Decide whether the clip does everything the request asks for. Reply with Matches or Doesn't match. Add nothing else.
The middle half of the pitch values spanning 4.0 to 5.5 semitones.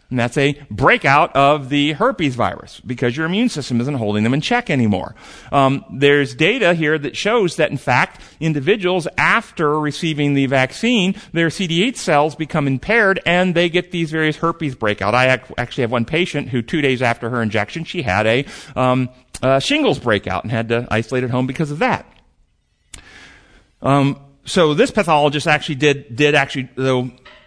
Matches